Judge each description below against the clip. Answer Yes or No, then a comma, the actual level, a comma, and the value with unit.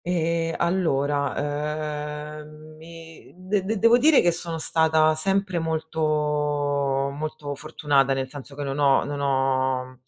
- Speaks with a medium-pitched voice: Yes, medium, 155 Hz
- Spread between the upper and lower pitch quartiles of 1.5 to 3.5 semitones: Yes, average, 2.7 semitones